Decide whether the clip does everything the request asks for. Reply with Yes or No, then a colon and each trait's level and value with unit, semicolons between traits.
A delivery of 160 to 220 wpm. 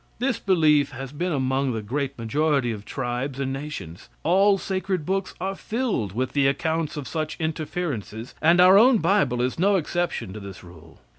Yes: average, 175 wpm